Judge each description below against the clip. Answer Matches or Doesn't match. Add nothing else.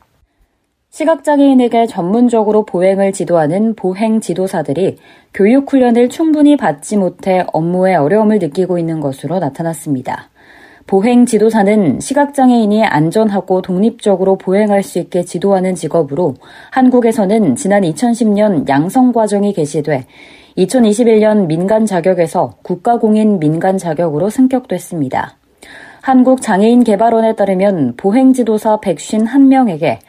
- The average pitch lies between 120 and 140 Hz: Doesn't match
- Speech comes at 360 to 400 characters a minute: Doesn't match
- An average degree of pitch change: Matches